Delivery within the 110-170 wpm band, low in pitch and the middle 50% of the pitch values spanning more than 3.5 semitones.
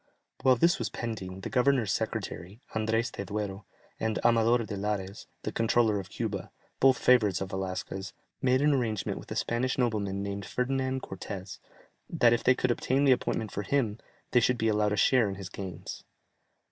No: average, 180 wpm; low, 110 Hz; average, 4.1 semitones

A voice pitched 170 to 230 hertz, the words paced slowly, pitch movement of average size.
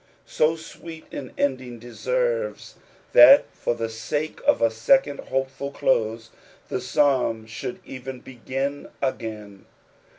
No: low, 130 Hz; slow, 120 wpm; average, 4.2 semitones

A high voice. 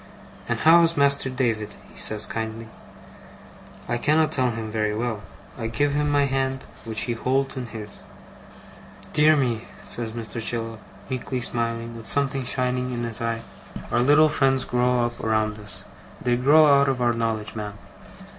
No: low, 120 Hz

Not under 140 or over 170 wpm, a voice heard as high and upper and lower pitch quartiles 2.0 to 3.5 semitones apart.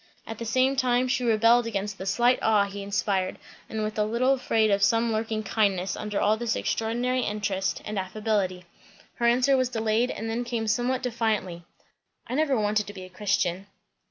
No: average, 185 wpm; high, 220 Hz; average, 3.0 semitones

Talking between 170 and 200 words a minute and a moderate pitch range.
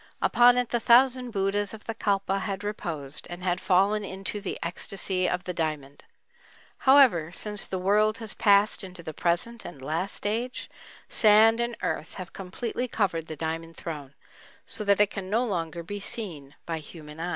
Yes: average, 175 wpm; average, 4.2 semitones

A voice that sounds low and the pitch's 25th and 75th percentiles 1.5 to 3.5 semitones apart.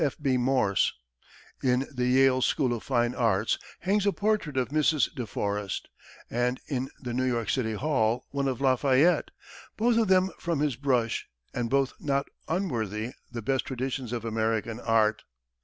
Yes: low, 130 Hz; average, 3.2 semitones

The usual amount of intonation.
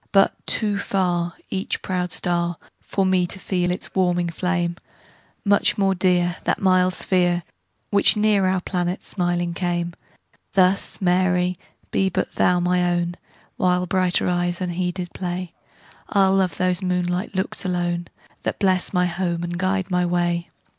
No: narrow, 1.2 semitones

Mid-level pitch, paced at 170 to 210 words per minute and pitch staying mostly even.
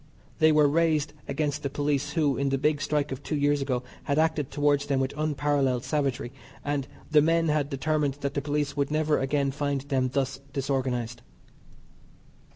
Yes: medium, 145 Hz; average, 175 wpm; narrow, 1.7 semitones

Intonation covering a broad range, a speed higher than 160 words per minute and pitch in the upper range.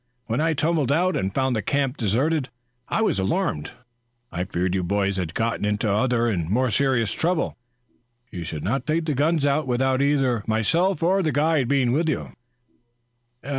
No: wide, 6.8 semitones; average, 175 wpm; low, 130 Hz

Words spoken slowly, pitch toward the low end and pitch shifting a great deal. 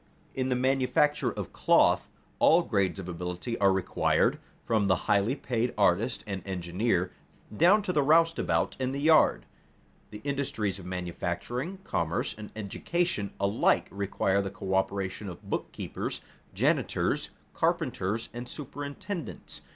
Yes: slow, 130 wpm; low, 105 Hz; wide, 6.5 semitones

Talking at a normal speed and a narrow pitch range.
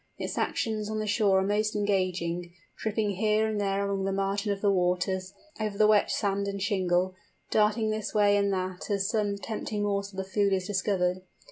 Yes: average, 195 wpm; narrow, 1.7 semitones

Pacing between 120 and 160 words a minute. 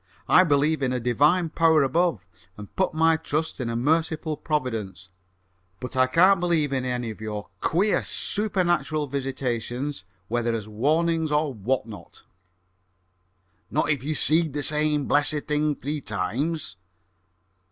Yes: average, 140 wpm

